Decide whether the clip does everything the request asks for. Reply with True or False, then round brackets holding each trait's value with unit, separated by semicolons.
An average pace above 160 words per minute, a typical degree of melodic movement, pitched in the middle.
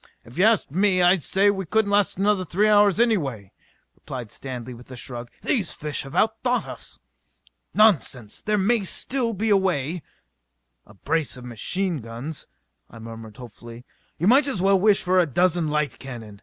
False (185 wpm; 8.6 semitones; 175 Hz)